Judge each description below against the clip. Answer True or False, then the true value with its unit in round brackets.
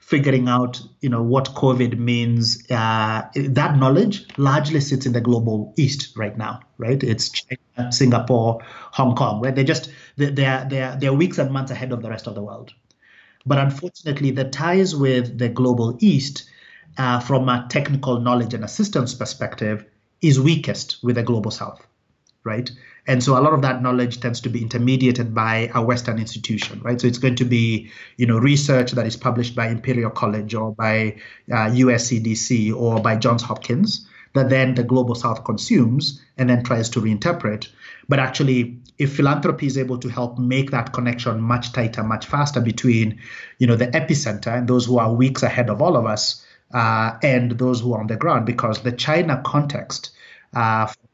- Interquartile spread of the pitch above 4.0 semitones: False (2.6 semitones)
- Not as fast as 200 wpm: True (185 wpm)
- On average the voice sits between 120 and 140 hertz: True (125 Hz)